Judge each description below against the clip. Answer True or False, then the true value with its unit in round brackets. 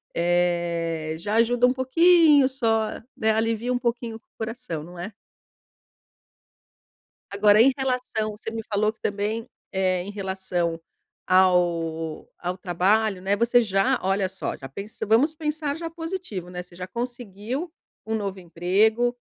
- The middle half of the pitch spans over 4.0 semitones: True (5.0 semitones)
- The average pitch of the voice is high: True (210 Hz)